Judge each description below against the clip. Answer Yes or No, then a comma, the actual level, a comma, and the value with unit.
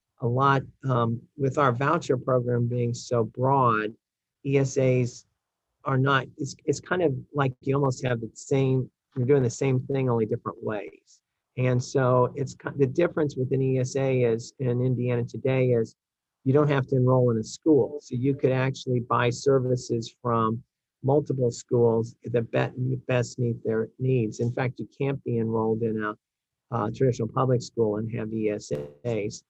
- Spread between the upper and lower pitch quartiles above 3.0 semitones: No, narrow, 2.6 semitones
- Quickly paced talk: No, average, 170 wpm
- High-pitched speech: No, low, 125 Hz